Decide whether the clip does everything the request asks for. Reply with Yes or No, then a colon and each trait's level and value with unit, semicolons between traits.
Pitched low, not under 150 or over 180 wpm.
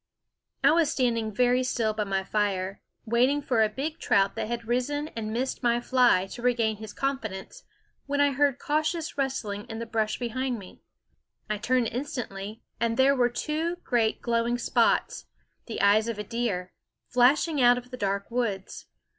No: high, 240 Hz; average, 170 wpm